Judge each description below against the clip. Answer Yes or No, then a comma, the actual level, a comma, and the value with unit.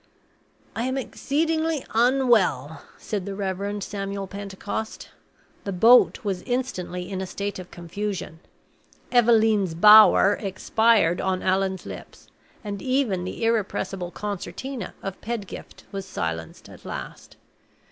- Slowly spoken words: Yes, slow, 115 wpm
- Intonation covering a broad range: No, average, 3.5 semitones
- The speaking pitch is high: Yes, high, 200 Hz